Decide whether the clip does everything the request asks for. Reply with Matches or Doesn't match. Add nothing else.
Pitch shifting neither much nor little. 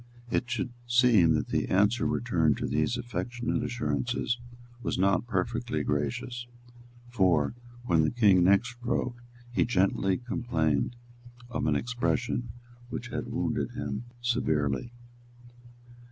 Doesn't match